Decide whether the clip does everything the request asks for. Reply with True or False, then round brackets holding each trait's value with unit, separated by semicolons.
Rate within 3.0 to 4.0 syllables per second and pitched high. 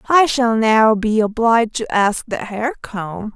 True (3.9 syllables/s; 225 Hz)